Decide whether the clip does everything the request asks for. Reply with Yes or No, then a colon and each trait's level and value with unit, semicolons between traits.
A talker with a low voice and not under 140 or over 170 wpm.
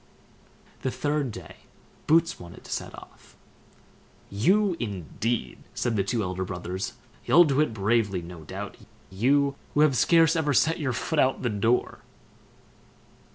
Yes: low, 120 Hz; average, 150 wpm